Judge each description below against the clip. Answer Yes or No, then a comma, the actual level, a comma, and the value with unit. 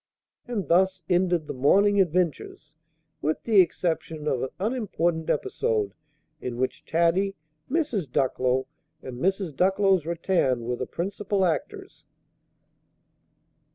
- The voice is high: No, medium, 170 Hz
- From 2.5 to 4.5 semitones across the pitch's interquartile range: No, wide, 5.5 semitones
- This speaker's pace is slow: Yes, slow, 115 wpm